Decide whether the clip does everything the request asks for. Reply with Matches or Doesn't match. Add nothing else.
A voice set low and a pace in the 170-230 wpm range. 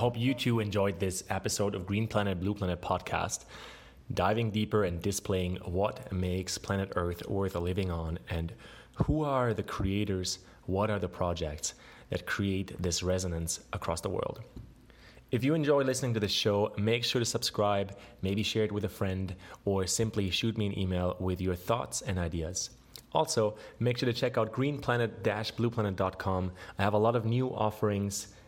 Matches